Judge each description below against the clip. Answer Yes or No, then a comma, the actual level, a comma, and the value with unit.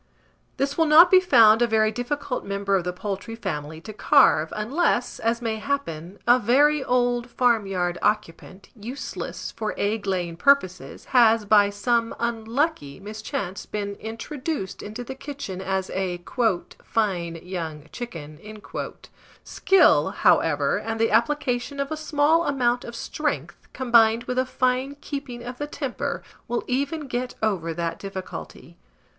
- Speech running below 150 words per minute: Yes, average, 140 wpm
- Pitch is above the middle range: Yes, high, 230 Hz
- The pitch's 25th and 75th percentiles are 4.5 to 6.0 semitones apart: Yes, average, 4.9 semitones